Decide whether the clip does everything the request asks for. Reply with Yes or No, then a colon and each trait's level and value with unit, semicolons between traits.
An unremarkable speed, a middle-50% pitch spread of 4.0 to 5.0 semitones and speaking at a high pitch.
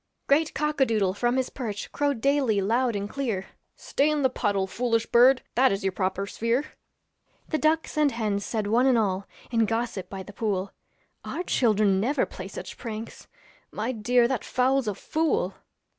Yes: average, 180 wpm; average, 4.6 semitones; high, 230 Hz